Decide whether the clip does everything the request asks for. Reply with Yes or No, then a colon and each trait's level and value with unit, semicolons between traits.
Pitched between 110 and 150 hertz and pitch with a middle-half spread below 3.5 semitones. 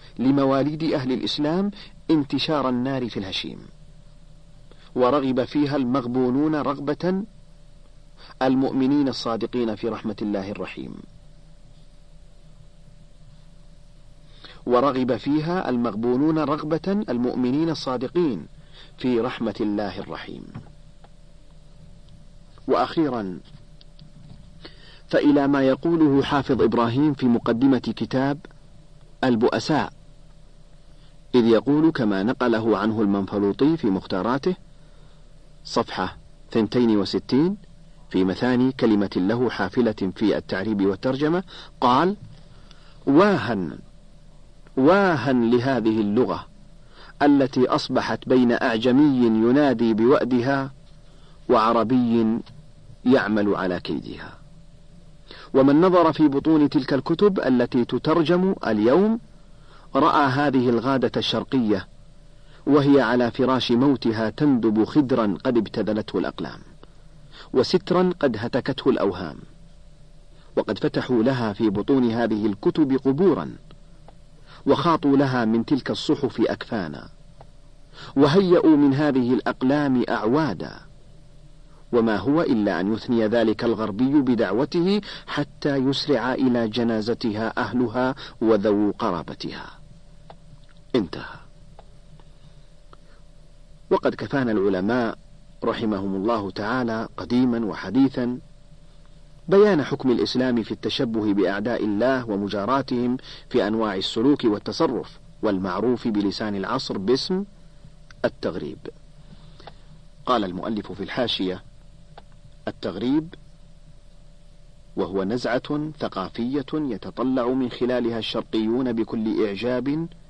No: medium, 140 Hz; average, 4.2 semitones